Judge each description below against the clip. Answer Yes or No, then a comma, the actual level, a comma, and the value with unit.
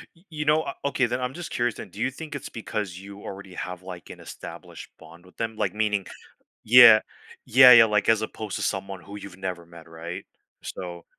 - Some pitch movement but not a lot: Yes, average, 4.9 semitones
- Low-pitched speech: Yes, low, 105 Hz